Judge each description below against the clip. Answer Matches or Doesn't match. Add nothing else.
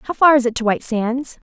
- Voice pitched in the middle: Doesn't match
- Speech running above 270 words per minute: Matches